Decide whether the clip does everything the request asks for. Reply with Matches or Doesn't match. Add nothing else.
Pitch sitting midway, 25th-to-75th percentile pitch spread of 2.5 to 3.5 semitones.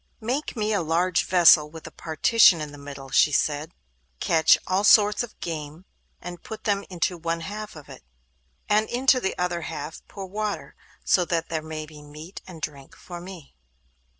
Doesn't match